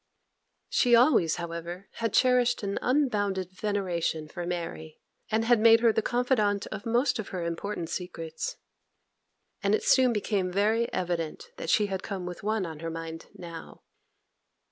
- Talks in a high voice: Yes, high, 200 Hz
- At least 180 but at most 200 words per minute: No, average, 155 wpm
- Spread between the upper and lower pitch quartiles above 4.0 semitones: Yes, average, 4.9 semitones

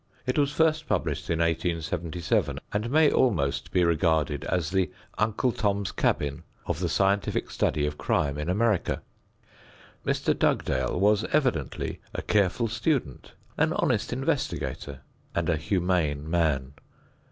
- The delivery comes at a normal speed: No, slow, 130 wpm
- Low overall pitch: Yes, very low, 90 Hz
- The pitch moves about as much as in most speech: No, wide, 6.2 semitones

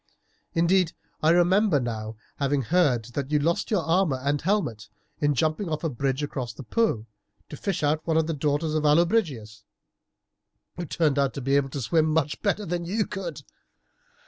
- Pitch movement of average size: Yes, average, 3.9 semitones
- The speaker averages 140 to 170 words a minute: No, average, 180 wpm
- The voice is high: No, medium, 155 Hz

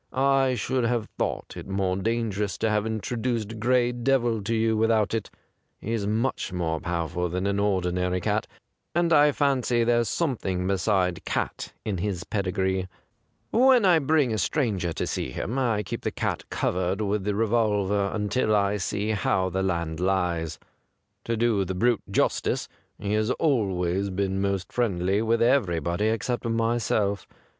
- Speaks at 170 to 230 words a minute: No, average, 160 wpm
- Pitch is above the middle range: No, low, 105 Hz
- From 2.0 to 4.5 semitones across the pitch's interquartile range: Yes, average, 3.9 semitones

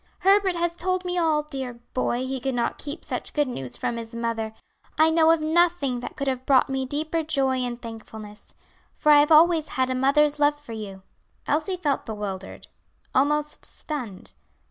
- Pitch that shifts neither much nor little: Yes, average, 4.6 semitones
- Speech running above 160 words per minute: Yes, average, 185 wpm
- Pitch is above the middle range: Yes, very high, 280 Hz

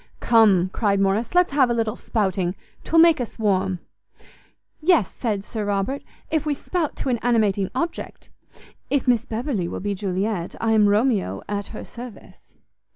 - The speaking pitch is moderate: No, high, 220 Hz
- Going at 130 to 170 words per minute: Yes, average, 160 wpm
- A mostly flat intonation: No, average, 4.3 semitones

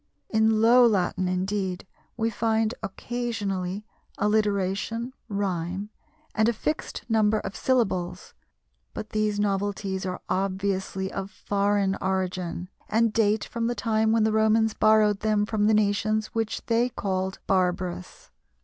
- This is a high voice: Yes, high, 210 Hz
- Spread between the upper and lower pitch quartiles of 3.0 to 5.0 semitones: No, narrow, 2.5 semitones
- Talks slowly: Yes, slow, 130 wpm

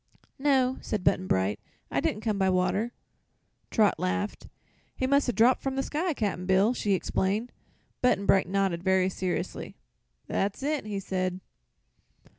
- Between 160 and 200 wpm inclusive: No, average, 150 wpm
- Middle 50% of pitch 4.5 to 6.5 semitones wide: Yes, average, 5.0 semitones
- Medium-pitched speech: No, high, 200 Hz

